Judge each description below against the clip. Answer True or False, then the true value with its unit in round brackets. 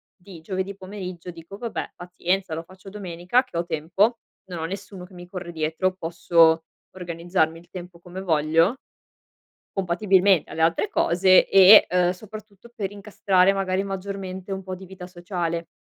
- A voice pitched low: False (185 Hz)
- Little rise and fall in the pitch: True (2.3 semitones)